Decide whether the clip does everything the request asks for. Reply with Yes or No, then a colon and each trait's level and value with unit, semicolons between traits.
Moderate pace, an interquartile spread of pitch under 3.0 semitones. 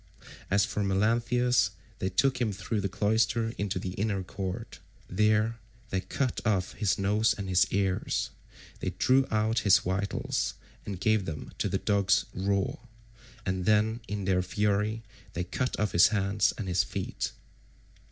Yes: average, 155 wpm; narrow, 2.6 semitones